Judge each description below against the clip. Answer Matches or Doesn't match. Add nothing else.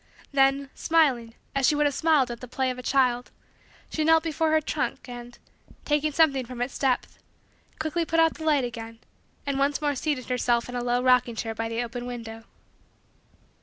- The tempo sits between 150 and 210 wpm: Matches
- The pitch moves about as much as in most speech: Matches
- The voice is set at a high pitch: Matches